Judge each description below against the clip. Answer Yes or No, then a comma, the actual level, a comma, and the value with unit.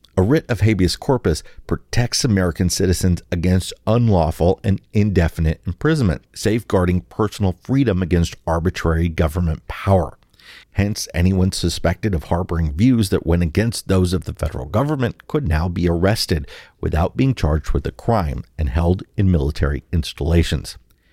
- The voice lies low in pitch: Yes, very low, 90 Hz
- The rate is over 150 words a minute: No, average, 140 wpm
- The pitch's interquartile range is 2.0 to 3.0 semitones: No, average, 3.7 semitones